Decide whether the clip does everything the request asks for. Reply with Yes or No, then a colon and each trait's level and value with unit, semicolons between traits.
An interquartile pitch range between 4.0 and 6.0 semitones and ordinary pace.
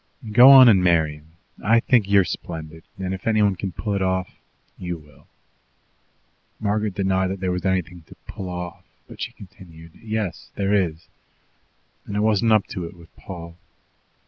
No: average, 3.1 semitones; average, 170 wpm